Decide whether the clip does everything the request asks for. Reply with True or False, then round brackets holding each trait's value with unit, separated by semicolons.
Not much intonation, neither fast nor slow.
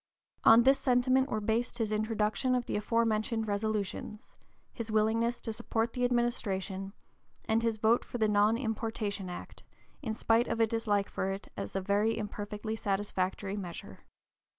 True (2.1 semitones; 155 wpm)